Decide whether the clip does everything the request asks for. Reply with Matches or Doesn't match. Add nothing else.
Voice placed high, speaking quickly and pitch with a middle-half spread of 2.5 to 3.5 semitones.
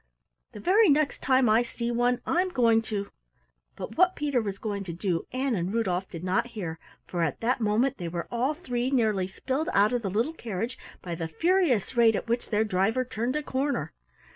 Doesn't match